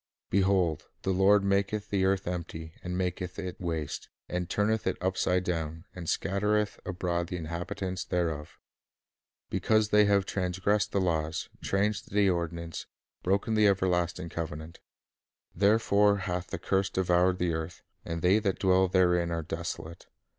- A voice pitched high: No, very low, 90 Hz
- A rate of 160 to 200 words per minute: No, average, 145 wpm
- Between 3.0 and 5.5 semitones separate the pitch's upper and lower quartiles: No, narrow, 2.5 semitones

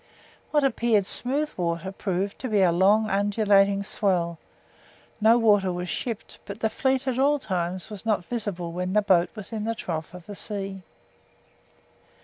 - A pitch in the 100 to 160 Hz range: No, high, 200 Hz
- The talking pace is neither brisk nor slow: Yes, average, 155 wpm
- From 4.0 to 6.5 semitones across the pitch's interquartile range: No, average, 3.4 semitones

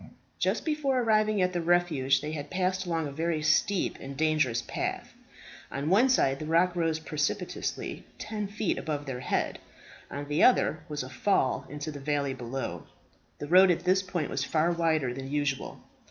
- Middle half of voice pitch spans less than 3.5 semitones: No, average, 4.2 semitones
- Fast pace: No, average, 180 wpm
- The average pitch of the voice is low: No, medium, 155 Hz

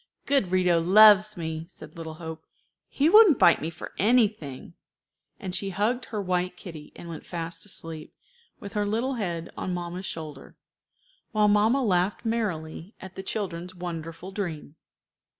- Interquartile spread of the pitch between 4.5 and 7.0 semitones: No, average, 4.1 semitones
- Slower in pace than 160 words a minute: Yes, average, 150 wpm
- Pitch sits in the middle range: Yes, medium, 180 Hz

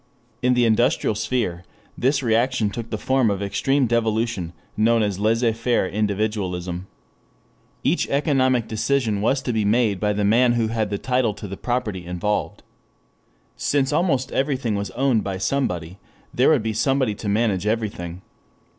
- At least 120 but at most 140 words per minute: No, average, 155 wpm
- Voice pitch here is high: No, low, 110 Hz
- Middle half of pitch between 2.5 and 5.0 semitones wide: Yes, average, 3.6 semitones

